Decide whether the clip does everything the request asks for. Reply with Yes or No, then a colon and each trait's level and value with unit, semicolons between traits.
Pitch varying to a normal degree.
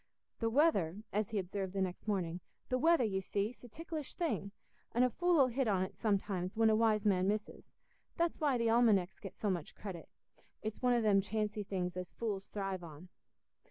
Yes: average, 3.8 semitones